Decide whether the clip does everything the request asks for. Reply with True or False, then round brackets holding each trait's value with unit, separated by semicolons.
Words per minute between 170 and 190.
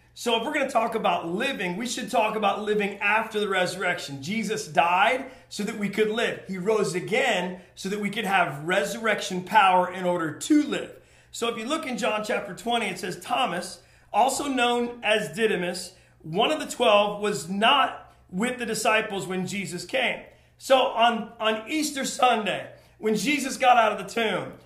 True (185 wpm)